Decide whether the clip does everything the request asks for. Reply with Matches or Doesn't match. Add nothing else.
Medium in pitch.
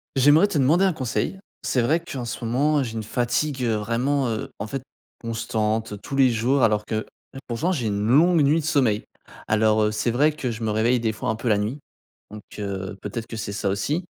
Doesn't match